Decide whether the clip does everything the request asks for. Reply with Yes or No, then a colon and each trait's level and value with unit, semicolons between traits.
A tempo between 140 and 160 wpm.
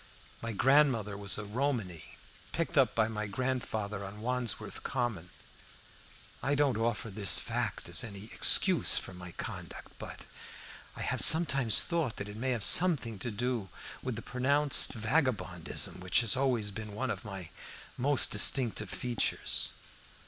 Yes: average, 150 wpm